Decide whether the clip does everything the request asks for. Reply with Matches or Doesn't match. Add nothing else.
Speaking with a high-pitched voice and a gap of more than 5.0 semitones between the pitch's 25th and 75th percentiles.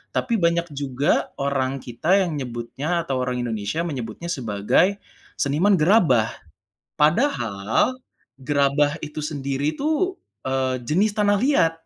Doesn't match